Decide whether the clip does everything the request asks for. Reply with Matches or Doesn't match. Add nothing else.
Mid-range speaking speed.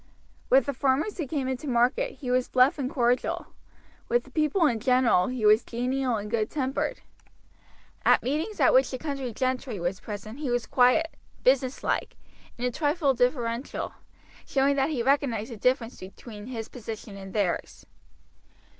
Matches